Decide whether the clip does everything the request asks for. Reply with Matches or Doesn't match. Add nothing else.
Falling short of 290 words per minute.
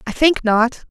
Matches